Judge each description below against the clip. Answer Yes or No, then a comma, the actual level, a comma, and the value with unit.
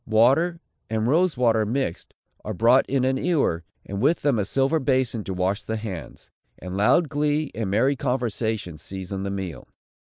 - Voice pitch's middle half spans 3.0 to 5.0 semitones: No, wide, 5.6 semitones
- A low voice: Yes, low, 115 Hz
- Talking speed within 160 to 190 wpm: Yes, average, 175 wpm